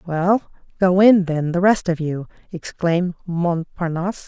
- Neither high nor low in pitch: Yes, medium, 175 Hz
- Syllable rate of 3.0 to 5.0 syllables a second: Yes, 4.3 syllables/s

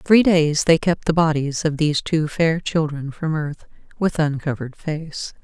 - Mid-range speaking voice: Yes, medium, 155 Hz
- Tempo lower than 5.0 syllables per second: Yes, 4.5 syllables/s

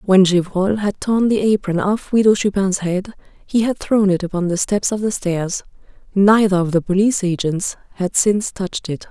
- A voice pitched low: No, high, 195 Hz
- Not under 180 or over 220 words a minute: Yes, average, 190 wpm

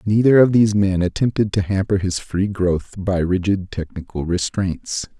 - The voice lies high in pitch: No, very low, 95 Hz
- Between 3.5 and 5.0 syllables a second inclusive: Yes, 4.6 syllables/s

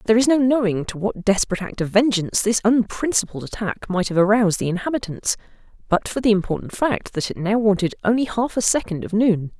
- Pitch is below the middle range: No, high, 210 Hz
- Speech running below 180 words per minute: No, fast, 205 wpm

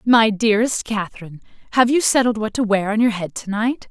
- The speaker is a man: No, female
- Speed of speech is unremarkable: No, fast, 215 wpm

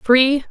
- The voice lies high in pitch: Yes, very high, 265 Hz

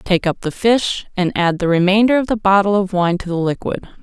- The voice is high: Yes, high, 195 Hz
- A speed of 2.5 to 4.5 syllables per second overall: No, 5.4 syllables/s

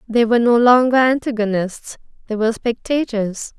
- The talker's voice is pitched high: Yes, high, 230 Hz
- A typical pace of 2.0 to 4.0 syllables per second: No, 5.2 syllables/s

